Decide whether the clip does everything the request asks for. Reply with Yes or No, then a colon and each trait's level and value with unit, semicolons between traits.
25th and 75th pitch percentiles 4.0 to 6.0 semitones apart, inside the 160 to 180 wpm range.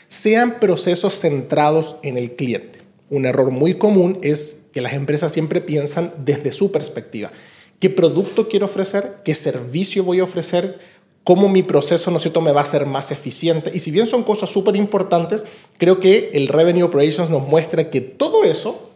Yes: average, 4.6 semitones; average, 175 wpm